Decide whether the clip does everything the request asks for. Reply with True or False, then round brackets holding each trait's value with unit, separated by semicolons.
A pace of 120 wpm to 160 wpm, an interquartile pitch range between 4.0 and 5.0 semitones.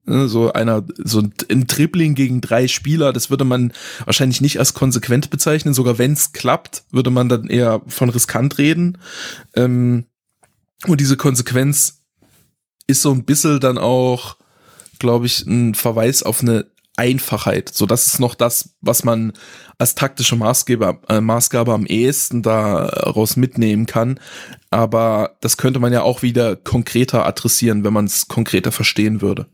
False (150 wpm; 2.8 semitones)